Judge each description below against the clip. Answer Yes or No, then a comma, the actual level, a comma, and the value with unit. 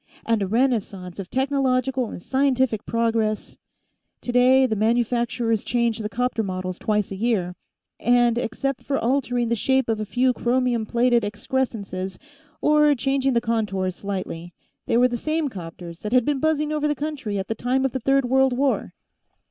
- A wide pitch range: No, average, 3.7 semitones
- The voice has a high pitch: Yes, high, 240 Hz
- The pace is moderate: Yes, average, 170 wpm